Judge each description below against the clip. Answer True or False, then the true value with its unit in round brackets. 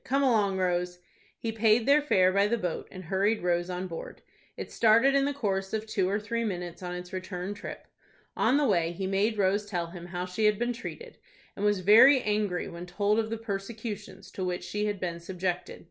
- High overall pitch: True (200 Hz)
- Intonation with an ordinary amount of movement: True (3.5 semitones)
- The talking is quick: True (215 wpm)